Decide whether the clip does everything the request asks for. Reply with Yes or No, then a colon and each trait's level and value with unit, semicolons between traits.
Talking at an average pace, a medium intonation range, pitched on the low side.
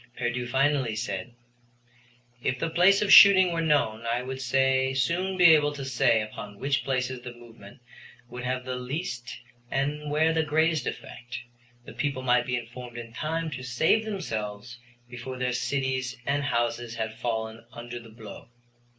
Yes: average, 160 wpm; average, 3.6 semitones; low, 130 Hz